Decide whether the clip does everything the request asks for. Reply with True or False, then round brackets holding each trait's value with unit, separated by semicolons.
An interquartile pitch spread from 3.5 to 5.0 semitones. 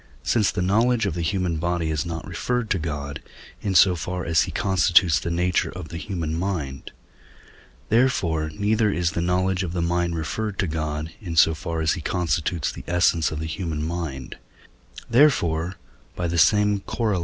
False (3.0 semitones)